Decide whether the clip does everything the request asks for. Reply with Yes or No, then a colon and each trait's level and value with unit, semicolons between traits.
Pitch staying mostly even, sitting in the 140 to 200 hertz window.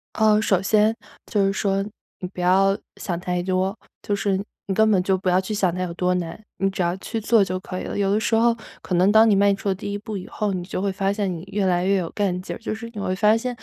Yes: narrow, 2.3 semitones; high, 195 Hz